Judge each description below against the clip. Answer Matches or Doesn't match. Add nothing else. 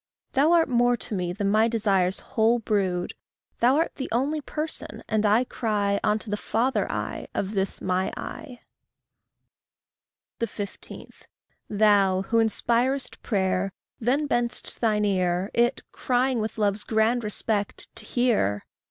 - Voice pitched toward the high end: Matches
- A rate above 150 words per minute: Doesn't match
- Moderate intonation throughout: Matches